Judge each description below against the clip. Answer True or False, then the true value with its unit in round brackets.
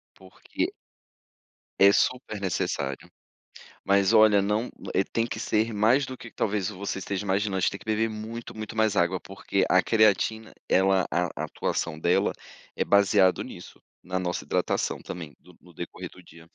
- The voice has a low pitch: True (100 Hz)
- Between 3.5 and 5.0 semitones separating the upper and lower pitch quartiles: False (2.8 semitones)